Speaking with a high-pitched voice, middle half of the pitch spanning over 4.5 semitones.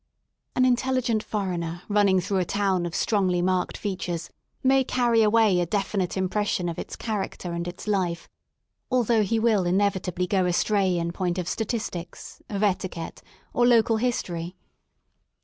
No: high, 195 Hz; average, 3.7 semitones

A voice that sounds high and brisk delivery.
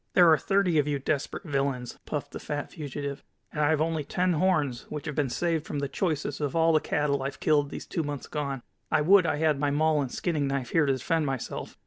No: medium, 150 Hz; fast, 240 wpm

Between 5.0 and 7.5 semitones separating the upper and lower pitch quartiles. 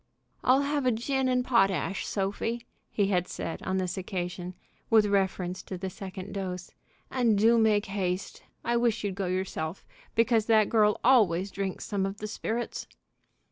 No: average, 3.5 semitones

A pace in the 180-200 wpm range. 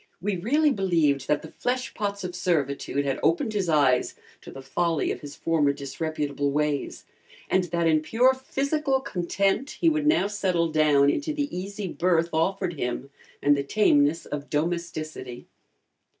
No: average, 155 wpm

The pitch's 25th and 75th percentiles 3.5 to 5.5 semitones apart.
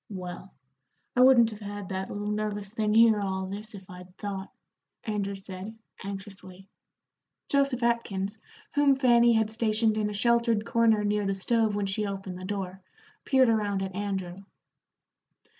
No: narrow, 2.6 semitones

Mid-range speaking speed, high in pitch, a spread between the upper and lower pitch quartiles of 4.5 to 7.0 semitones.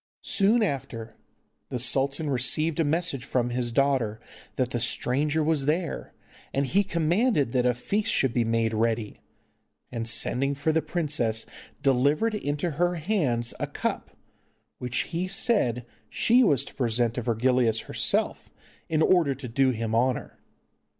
No: average, 150 wpm; low, 135 Hz; average, 5.2 semitones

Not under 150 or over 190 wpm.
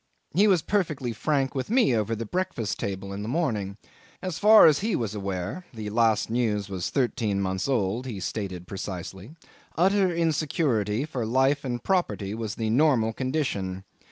Yes: average, 165 wpm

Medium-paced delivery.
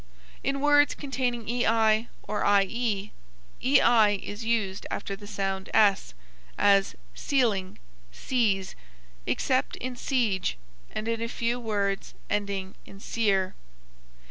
No: slow, 115 wpm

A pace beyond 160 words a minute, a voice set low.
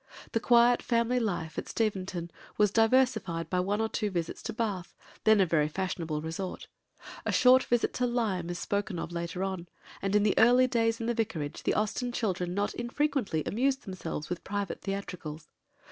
No: average, 180 wpm; high, 200 Hz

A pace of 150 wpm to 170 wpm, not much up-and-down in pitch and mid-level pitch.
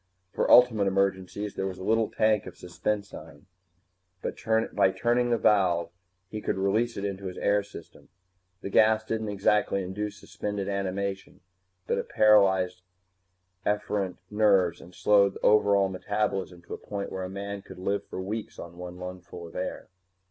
No: average, 160 wpm; narrow, 2.1 semitones; low, 100 Hz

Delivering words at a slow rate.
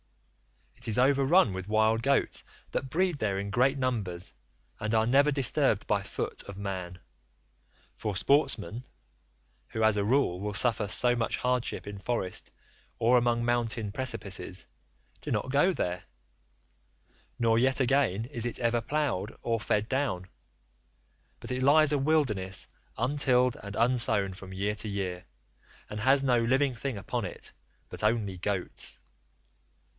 No: average, 145 wpm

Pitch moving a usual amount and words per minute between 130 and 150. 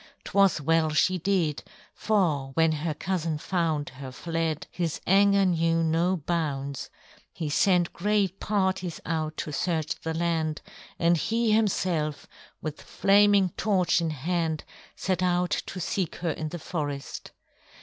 Yes: average, 3.2 semitones; average, 140 wpm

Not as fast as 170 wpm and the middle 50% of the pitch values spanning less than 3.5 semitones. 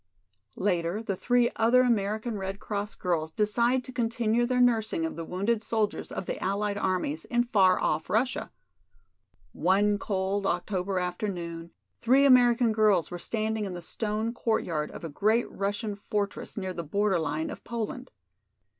No: average, 155 wpm; average, 3.8 semitones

